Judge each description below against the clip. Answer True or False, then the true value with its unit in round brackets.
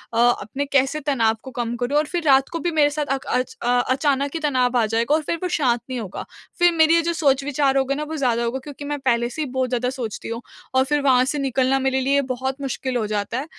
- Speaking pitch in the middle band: False (265 Hz)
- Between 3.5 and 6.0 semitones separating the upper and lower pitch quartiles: False (2.9 semitones)